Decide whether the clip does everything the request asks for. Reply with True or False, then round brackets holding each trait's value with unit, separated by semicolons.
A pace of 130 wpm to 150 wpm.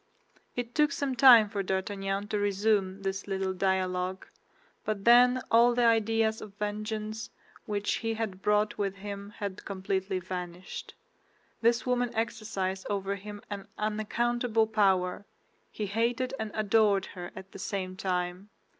True (140 wpm)